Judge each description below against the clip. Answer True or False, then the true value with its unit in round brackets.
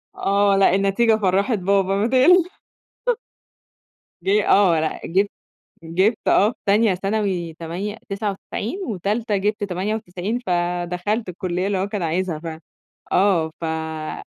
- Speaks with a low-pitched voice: False (195 Hz)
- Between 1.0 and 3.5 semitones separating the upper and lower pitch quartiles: True (3.0 semitones)